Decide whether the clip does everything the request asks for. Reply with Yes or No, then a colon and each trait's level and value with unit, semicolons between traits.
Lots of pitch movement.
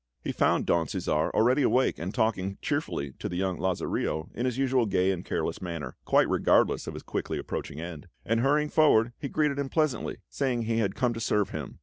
Yes: wide, 6.3 semitones